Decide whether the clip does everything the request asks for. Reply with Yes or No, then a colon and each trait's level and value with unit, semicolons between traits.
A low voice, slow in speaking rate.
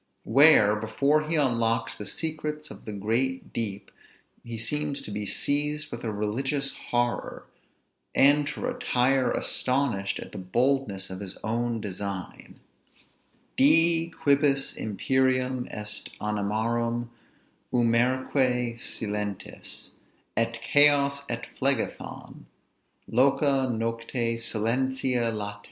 Yes: low, 120 Hz; slow, 105 wpm